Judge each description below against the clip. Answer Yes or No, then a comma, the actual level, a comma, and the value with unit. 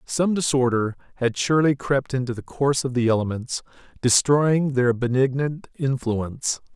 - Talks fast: No, slow, 135 wpm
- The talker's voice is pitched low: Yes, low, 130 Hz